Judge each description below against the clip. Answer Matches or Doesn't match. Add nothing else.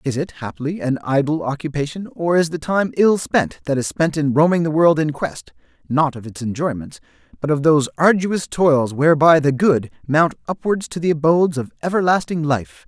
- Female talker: Doesn't match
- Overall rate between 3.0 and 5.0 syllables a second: Doesn't match